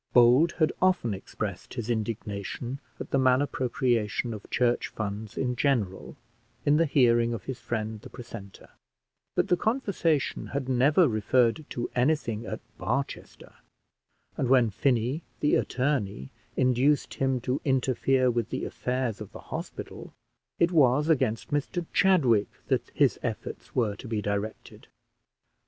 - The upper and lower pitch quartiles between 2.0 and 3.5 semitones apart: No, average, 3.9 semitones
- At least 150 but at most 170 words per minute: No, average, 140 wpm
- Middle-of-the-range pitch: No, low, 125 Hz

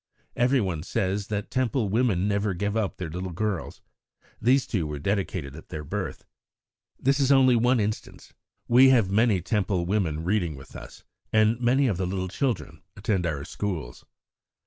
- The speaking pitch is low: Yes, low, 100 Hz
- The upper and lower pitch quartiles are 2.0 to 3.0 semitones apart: No, average, 4.8 semitones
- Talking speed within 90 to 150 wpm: No, average, 165 wpm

